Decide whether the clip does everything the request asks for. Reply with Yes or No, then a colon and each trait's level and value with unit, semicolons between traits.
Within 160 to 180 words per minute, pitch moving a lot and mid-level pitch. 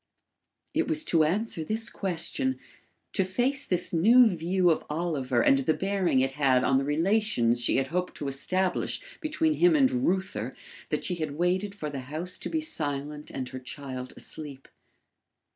Yes: average, 170 wpm; wide, 6.4 semitones; medium, 170 Hz